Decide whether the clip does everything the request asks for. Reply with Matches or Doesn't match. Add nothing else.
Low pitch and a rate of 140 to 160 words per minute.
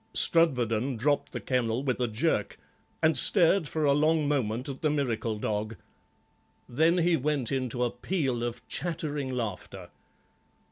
Matches